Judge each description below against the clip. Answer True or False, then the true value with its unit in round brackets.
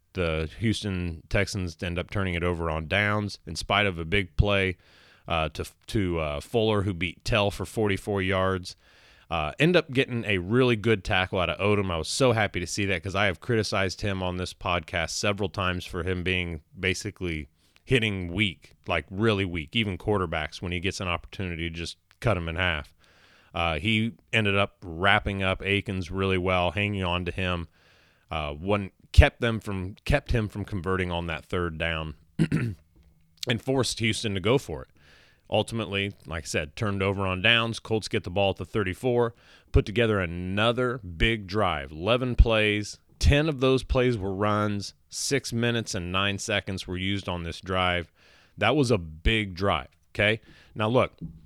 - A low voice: True (95 Hz)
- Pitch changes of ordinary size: True (3.5 semitones)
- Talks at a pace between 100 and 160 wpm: False (185 wpm)